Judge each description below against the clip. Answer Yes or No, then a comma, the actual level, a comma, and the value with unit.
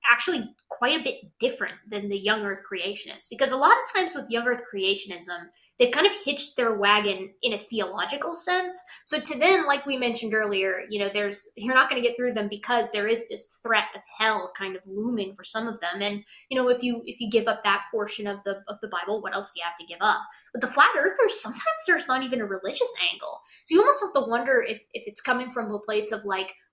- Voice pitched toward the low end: No, high, 225 Hz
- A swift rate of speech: Yes, fast, 245 wpm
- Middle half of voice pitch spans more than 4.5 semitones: Yes, average, 5.0 semitones